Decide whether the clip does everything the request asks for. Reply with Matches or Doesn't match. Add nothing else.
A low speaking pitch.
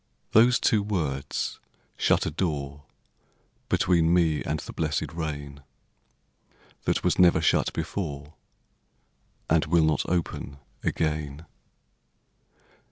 Matches